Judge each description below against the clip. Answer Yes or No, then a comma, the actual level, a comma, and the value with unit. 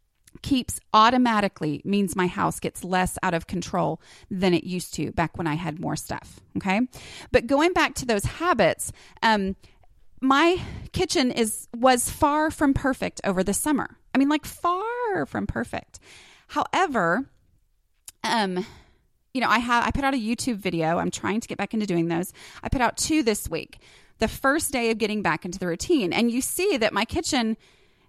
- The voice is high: Yes, high, 230 Hz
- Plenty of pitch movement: Yes, wide, 6.5 semitones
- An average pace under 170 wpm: No, average, 180 wpm